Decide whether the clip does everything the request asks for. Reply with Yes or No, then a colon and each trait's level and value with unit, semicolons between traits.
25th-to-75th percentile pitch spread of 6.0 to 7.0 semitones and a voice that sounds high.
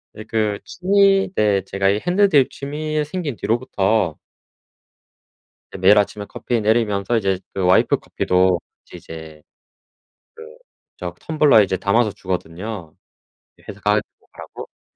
No: wide, 6.3 semitones; low, 105 Hz